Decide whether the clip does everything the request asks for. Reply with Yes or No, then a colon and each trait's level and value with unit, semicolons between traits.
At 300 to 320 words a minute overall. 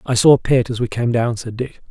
Yes: fast, 315 wpm